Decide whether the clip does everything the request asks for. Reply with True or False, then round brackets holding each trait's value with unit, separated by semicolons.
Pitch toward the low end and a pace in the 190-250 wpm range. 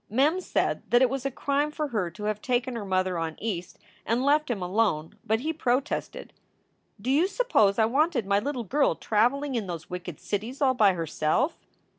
False (235 Hz; 195 wpm)